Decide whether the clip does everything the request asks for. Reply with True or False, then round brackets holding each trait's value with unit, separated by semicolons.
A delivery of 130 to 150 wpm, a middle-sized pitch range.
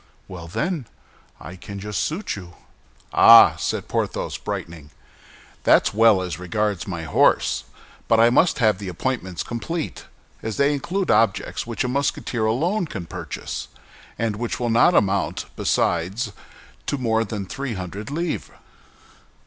False (140 wpm; 5.8 semitones)